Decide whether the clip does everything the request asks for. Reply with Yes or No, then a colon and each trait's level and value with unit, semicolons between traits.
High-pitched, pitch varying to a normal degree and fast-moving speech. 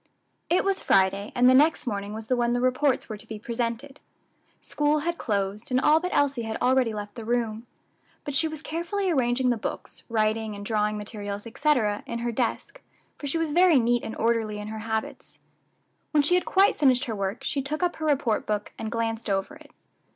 Yes: high, 240 Hz; average, 4.9 semitones; fast, 210 wpm